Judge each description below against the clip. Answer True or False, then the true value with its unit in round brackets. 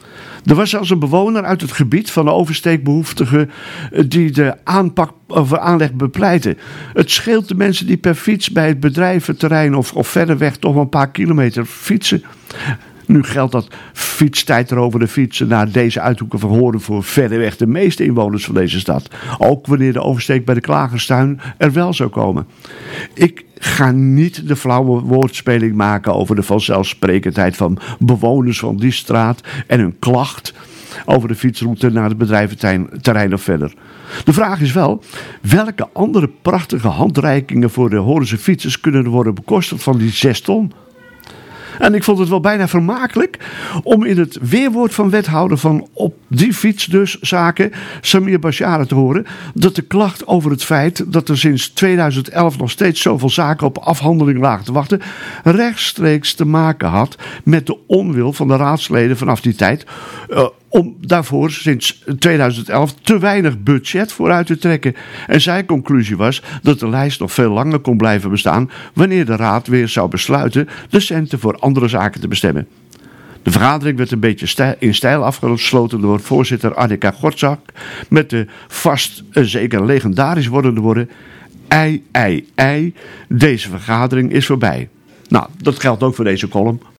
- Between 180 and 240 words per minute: False (170 wpm)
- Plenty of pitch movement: True (5.9 semitones)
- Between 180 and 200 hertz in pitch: False (140 Hz)